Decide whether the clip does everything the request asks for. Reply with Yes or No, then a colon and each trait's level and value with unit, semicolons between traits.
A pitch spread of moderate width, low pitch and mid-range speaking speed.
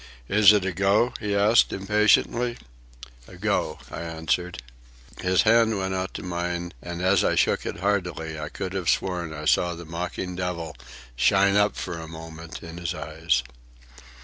Yes: average, 3.2 semitones; very low, 90 Hz; average, 170 wpm